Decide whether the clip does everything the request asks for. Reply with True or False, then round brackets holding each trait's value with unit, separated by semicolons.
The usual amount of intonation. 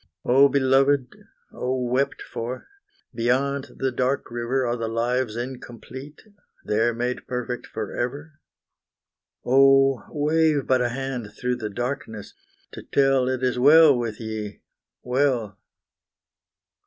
False (2.3 semitones)